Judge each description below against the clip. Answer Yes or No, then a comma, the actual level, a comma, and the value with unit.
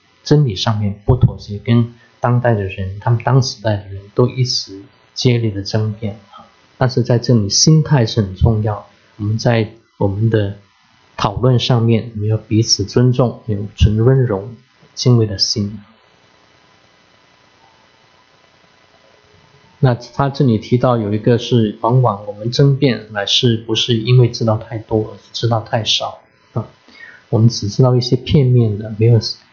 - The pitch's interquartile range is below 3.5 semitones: Yes, average, 2.9 semitones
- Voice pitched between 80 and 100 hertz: No, low, 115 Hz